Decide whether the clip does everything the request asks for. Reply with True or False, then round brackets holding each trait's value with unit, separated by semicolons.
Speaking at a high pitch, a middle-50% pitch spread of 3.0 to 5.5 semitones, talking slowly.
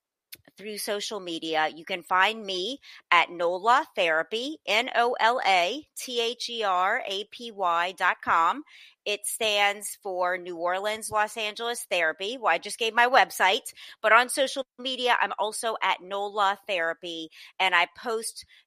True (205 Hz; 4.4 semitones; 125 wpm)